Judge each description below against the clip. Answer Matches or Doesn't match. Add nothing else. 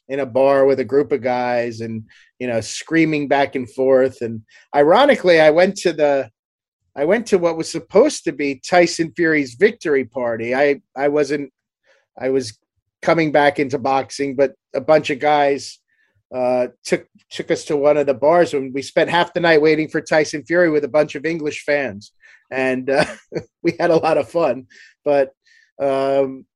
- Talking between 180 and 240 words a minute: Matches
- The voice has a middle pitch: Matches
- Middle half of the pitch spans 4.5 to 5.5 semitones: Doesn't match